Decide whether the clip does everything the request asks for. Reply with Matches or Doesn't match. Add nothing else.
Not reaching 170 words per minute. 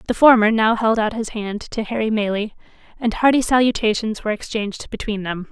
Doesn't match